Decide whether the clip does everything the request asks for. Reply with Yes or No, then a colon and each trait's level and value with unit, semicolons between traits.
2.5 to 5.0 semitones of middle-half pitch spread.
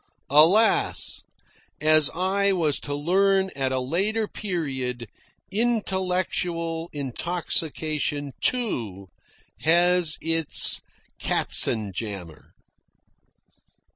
No: wide, 5.5 semitones